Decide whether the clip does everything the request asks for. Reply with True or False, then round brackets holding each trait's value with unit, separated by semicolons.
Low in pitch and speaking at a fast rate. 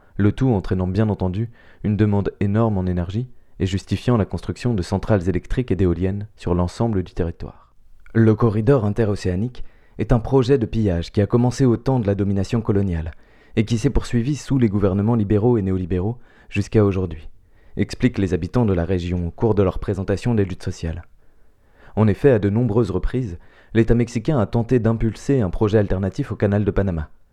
False (105 Hz; 185 wpm)